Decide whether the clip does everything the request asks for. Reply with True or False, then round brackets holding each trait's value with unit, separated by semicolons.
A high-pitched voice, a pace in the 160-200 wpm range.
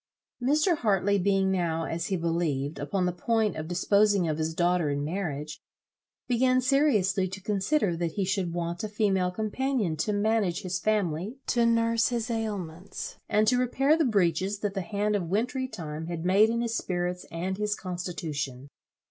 True (195 Hz; 175 wpm)